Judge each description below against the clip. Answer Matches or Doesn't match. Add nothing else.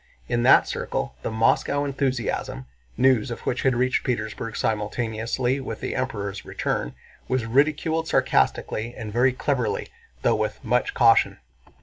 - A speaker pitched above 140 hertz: Doesn't match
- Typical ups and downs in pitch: Matches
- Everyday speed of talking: Doesn't match